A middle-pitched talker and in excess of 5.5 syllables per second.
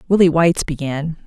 Yes: medium, 160 Hz; 5.8 syllables/s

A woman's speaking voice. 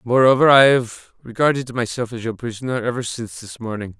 No: male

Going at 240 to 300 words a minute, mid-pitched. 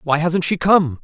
No: fast, 230 wpm; medium, 165 Hz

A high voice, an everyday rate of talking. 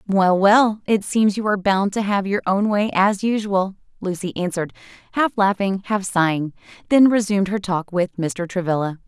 Yes: high, 195 Hz; average, 180 wpm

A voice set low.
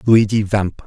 Yes: low, 105 Hz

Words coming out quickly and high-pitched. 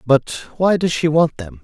No: fast, 220 wpm; medium, 150 Hz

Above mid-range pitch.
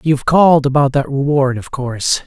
No: medium, 140 Hz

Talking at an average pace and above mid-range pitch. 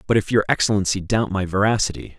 No: average, 190 wpm; low, 100 Hz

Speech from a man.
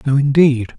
Yes: male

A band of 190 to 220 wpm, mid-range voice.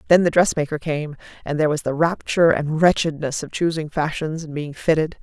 Yes: average, 195 wpm; medium, 155 Hz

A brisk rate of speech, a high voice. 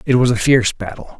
No: fast, 250 wpm; low, 120 Hz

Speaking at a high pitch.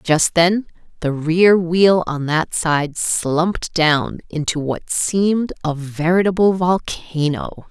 No: medium, 170 Hz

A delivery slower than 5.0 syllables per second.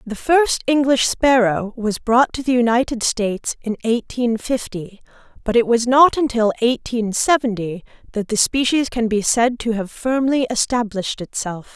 Yes: 4.5 syllables/s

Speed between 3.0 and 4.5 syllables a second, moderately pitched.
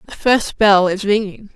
No: 4.3 syllables/s; high, 205 Hz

